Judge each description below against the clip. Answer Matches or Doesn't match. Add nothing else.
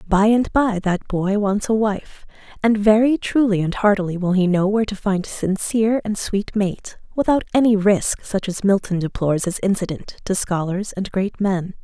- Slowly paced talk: Doesn't match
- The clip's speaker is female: Matches